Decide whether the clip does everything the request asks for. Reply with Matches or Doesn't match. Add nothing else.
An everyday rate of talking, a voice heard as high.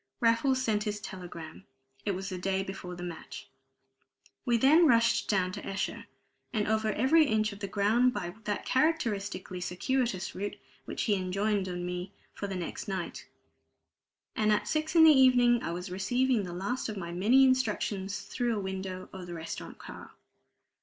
Matches